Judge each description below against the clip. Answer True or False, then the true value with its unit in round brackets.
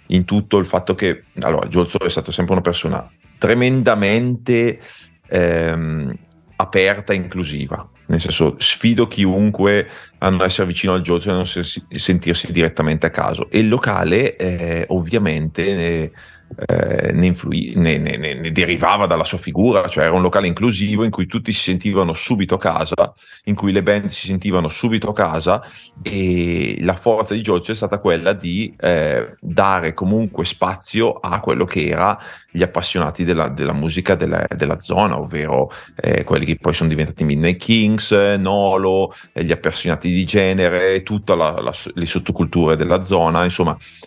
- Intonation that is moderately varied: True (3.3 semitones)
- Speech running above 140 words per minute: True (160 wpm)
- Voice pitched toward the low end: True (90 Hz)